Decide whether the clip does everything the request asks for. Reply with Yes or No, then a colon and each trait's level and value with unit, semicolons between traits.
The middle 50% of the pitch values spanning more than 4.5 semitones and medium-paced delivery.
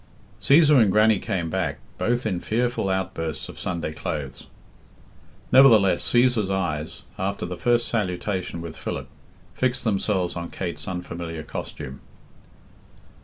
No: average, 5.0 semitones; slow, 120 wpm